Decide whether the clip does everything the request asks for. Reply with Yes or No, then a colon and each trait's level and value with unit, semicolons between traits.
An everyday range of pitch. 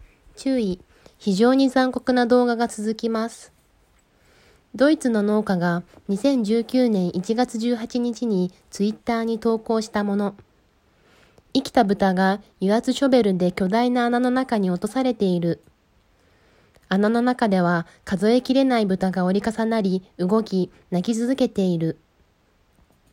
Yes: average, 4.6 semitones